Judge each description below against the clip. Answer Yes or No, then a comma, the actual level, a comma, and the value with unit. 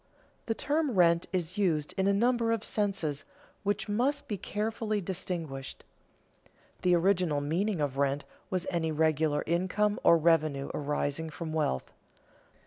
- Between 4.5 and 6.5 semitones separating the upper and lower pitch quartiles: Yes, average, 5.0 semitones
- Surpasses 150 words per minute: No, slow, 135 wpm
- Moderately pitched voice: Yes, medium, 175 Hz